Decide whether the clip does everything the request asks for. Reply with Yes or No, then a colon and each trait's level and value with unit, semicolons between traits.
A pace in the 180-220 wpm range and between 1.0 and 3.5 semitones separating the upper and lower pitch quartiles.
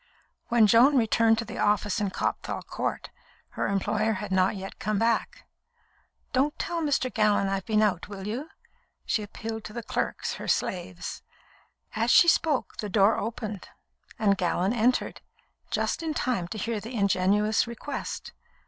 No: average, 155 wpm; average, 2.9 semitones